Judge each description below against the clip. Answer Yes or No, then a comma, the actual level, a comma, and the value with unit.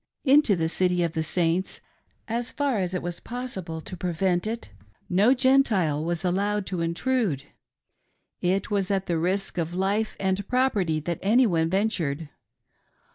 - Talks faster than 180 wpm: No, average, 145 wpm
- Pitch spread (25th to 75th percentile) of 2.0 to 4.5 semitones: Yes, average, 4.2 semitones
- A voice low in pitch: No, medium, 185 Hz